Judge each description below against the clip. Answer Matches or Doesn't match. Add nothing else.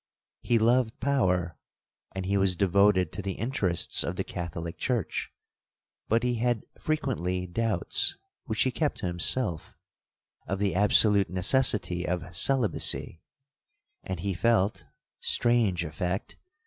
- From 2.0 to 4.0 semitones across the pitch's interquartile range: Doesn't match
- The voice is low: Matches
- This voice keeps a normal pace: Doesn't match